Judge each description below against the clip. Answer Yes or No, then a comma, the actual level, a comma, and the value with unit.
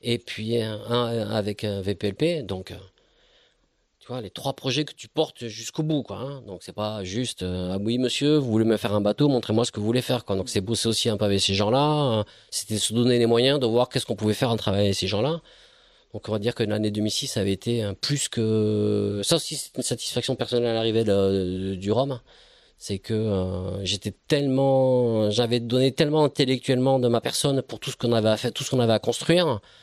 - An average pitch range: Yes, average, 3.9 semitones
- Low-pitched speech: Yes, low, 115 Hz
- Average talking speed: No, fast, 225 wpm